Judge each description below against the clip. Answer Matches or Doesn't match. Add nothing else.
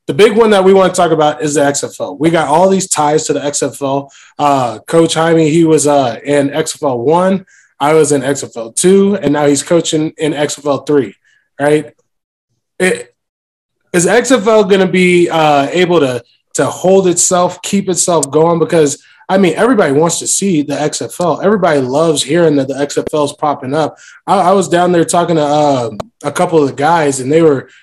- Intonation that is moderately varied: Matches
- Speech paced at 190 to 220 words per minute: Matches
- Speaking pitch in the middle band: Matches